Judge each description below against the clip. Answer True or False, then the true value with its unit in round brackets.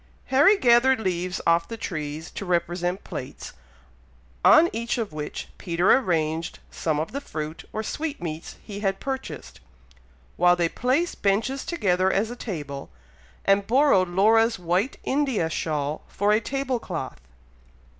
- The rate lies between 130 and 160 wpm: True (140 wpm)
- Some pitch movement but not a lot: False (6.2 semitones)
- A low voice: False (195 Hz)